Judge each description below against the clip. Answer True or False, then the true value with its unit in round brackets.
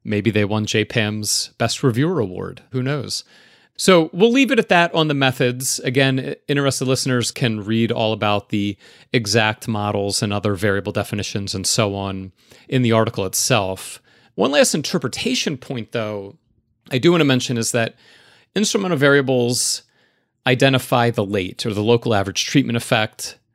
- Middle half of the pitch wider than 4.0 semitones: True (4.4 semitones)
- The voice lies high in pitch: False (120 Hz)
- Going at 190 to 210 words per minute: False (160 wpm)